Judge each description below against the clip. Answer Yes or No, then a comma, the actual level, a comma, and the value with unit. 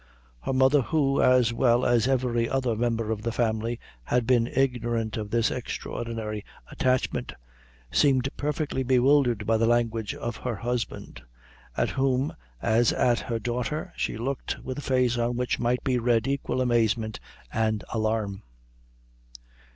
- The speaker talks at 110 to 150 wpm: Yes, average, 145 wpm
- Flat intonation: Yes, narrow, 2.1 semitones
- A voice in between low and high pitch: No, low, 120 Hz